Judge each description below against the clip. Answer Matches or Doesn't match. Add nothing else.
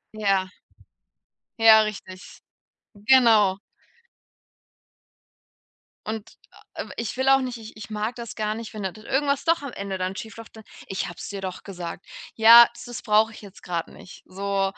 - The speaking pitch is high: Matches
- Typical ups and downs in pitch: Matches